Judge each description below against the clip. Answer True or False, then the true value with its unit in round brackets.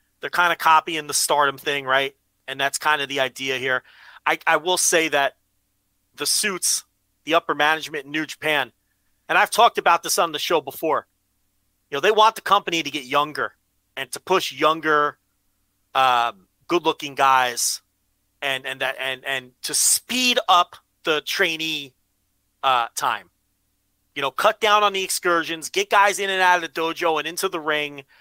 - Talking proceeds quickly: False (180 wpm)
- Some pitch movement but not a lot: False (8.4 semitones)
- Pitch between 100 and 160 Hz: True (140 Hz)